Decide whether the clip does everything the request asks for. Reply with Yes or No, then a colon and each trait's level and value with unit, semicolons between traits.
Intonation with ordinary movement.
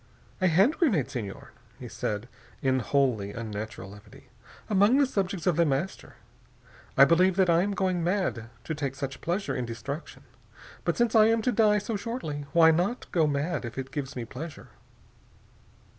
No: wide, 6.9 semitones